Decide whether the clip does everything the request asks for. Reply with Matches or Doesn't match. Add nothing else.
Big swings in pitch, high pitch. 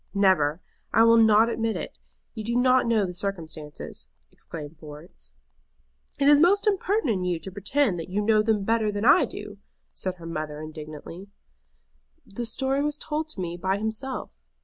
Matches